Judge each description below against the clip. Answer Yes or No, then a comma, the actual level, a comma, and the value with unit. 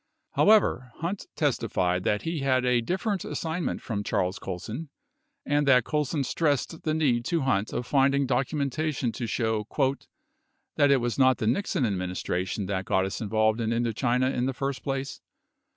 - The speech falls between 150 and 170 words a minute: Yes, average, 165 wpm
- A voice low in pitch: Yes, low, 130 Hz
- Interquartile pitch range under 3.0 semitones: No, average, 4.7 semitones